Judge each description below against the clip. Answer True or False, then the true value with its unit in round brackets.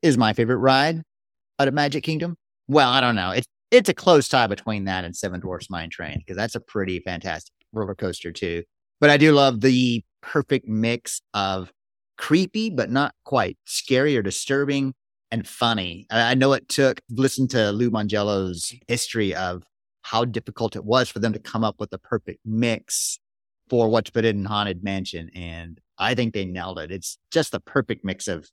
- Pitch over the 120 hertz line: False (115 Hz)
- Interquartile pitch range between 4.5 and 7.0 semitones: True (5.3 semitones)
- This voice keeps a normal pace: True (190 wpm)